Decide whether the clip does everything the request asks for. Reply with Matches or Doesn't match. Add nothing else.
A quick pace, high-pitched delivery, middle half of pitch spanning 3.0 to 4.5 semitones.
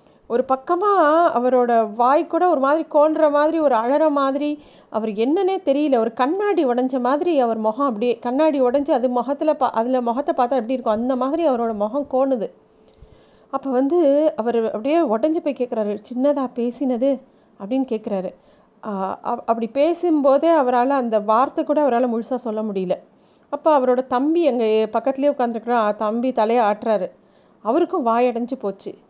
Matches